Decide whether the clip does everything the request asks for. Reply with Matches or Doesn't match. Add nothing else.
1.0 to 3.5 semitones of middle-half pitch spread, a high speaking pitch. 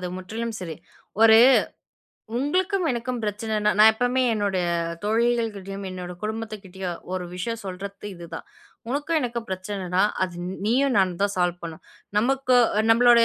Doesn't match